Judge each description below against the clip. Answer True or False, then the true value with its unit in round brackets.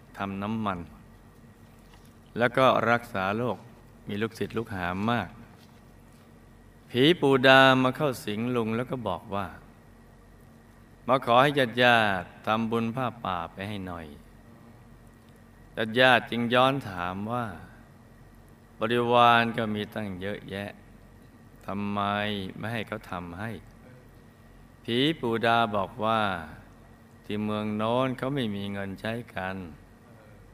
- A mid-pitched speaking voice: False (115 Hz)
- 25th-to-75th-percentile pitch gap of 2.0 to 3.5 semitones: True (2.8 semitones)